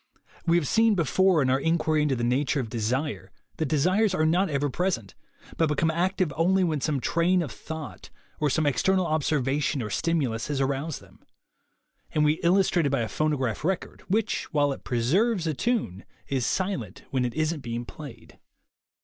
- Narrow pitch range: No, average, 4.4 semitones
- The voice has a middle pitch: Yes, medium, 155 Hz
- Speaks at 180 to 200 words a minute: Yes, average, 185 wpm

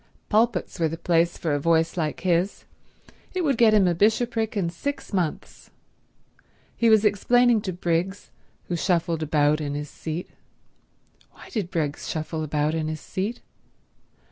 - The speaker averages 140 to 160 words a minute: Yes, average, 150 wpm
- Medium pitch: Yes, medium, 175 Hz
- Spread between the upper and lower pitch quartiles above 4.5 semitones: Yes, average, 4.9 semitones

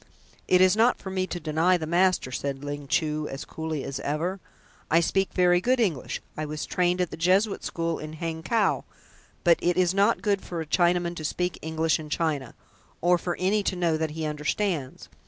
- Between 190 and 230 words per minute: Yes, average, 200 wpm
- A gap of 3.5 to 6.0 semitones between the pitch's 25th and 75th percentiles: No, average, 3.0 semitones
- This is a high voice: No, medium, 170 Hz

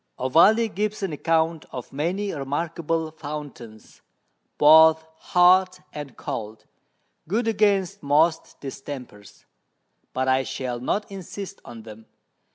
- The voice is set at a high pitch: No, medium, 160 Hz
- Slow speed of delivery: Yes, slow, 110 wpm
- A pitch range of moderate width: No, wide, 5.9 semitones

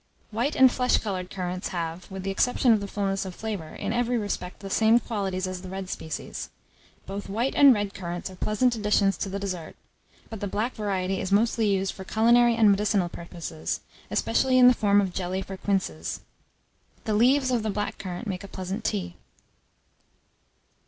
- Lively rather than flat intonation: No, average, 3.1 semitones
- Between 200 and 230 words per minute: No, average, 185 wpm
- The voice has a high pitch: Yes, high, 200 Hz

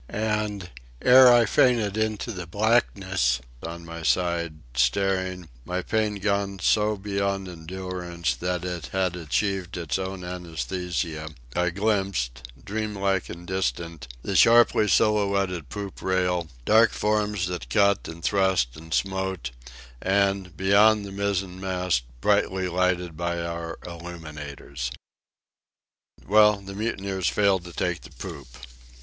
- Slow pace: Yes, slow, 125 wpm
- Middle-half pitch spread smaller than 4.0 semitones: Yes, average, 2.8 semitones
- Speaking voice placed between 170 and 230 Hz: No, very low, 95 Hz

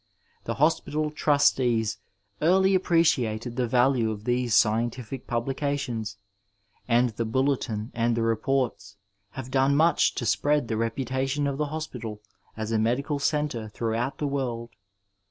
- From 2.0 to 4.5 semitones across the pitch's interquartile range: Yes, average, 3.8 semitones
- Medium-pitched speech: No, low, 125 Hz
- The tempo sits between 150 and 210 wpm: No, slow, 135 wpm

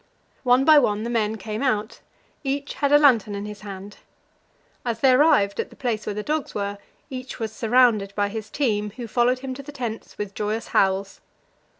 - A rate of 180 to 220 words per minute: Yes, average, 200 wpm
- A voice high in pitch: Yes, high, 225 Hz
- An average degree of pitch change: Yes, average, 3.8 semitones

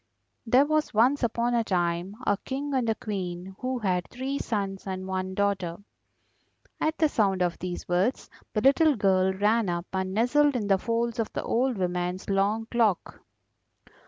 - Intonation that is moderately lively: Yes, average, 4.5 semitones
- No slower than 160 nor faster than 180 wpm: Yes, average, 170 wpm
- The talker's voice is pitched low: No, high, 205 Hz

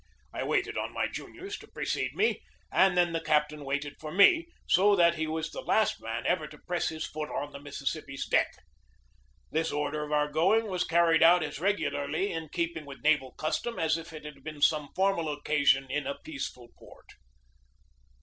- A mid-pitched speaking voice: Yes, medium, 155 Hz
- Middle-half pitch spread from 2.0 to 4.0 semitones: Yes, average, 3.3 semitones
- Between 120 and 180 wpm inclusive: No, average, 190 wpm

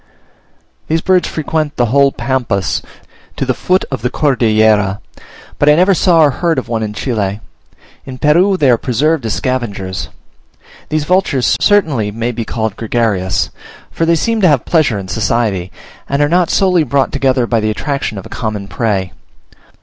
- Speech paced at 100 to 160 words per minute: No, average, 175 wpm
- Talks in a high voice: No, low, 130 Hz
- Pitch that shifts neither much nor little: No, wide, 6.1 semitones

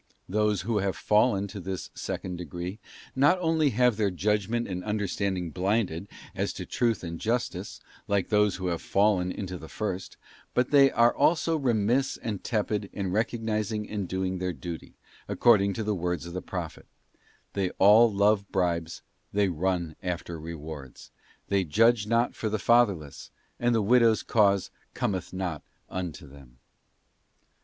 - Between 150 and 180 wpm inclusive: Yes, average, 155 wpm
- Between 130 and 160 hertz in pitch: No, low, 100 Hz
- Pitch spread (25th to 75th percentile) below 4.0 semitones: Yes, average, 3.6 semitones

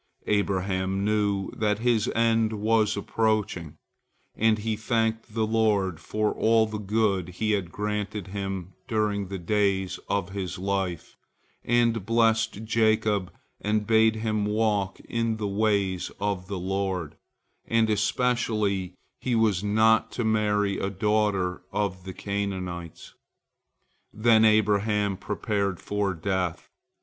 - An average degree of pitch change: No, narrow, 2.2 semitones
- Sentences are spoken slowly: Yes, slow, 125 wpm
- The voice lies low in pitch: Yes, low, 105 Hz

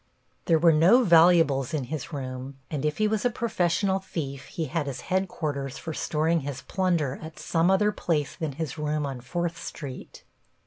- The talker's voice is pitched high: No, medium, 160 Hz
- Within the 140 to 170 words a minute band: No, average, 180 wpm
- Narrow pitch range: No, average, 3.9 semitones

